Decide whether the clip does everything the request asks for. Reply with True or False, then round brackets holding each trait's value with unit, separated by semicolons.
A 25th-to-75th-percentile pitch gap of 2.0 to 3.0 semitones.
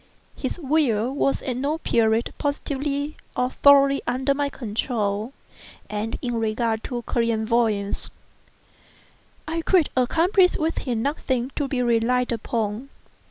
False (3.8 semitones)